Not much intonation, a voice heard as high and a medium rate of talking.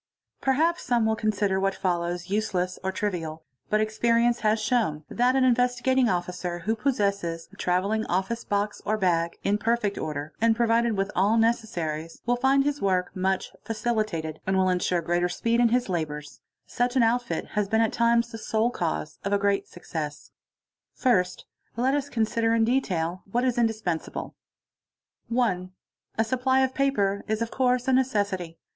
No: average, 4.7 semitones; high, 215 Hz; average, 175 wpm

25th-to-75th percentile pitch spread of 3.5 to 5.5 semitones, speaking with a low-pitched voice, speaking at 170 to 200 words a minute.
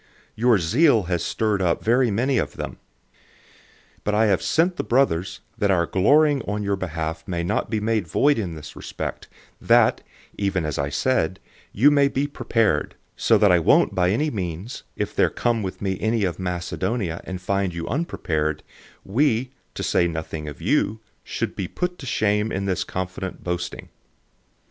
Yes: average, 5.0 semitones; low, 100 Hz; average, 175 wpm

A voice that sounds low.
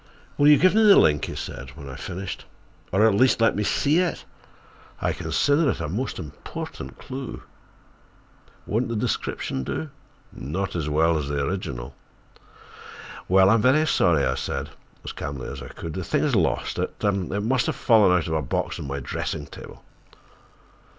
Yes: very low, 95 Hz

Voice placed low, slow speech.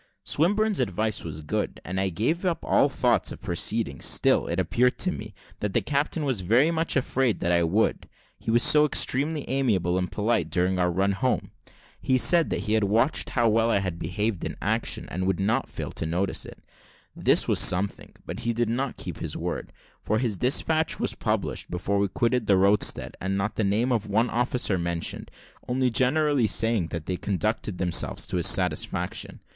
No: low, 110 Hz; average, 195 wpm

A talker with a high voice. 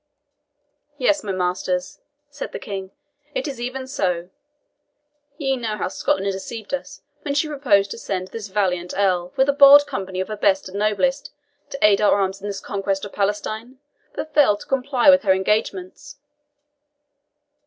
Yes: high, 210 Hz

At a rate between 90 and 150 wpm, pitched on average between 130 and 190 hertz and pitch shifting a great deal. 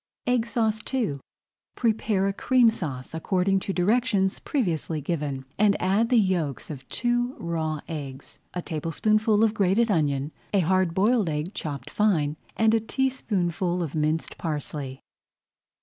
Yes: average, 140 wpm; medium, 185 Hz; wide, 6.0 semitones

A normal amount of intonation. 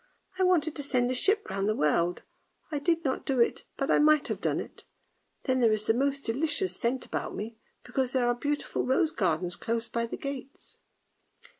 Yes: average, 4.2 semitones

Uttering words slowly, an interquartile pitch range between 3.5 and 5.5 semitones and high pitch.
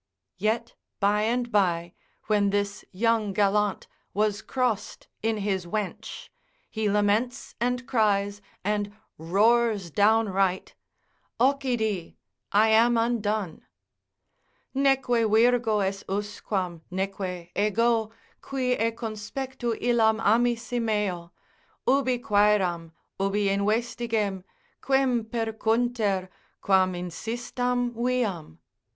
No: slow, 90 wpm; average, 3.1 semitones; high, 215 Hz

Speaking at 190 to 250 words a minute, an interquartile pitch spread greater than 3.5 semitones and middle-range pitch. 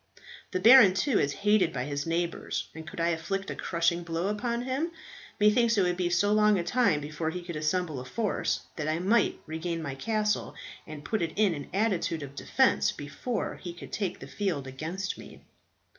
Yes: average, 200 wpm; average, 4.8 semitones; medium, 175 Hz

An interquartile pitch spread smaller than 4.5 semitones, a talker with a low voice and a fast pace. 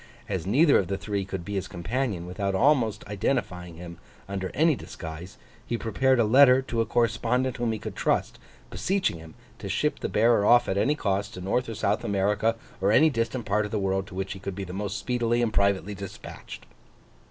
Yes: average, 3.8 semitones; low, 105 Hz; fast, 210 wpm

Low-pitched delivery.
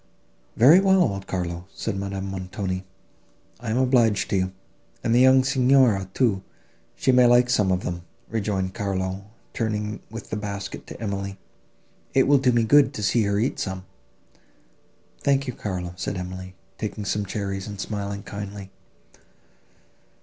Yes: low, 100 Hz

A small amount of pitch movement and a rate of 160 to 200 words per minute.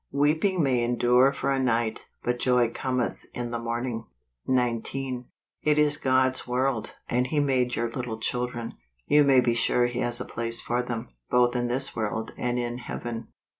Yes: narrow, 1.7 semitones; average, 180 wpm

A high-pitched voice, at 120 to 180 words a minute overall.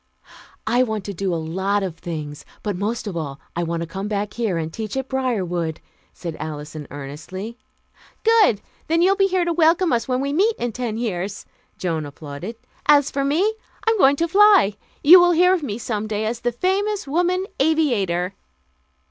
No: high, 225 Hz; average, 190 wpm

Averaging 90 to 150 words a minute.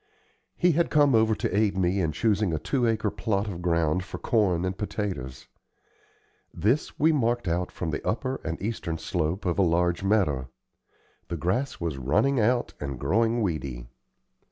No: average, 170 wpm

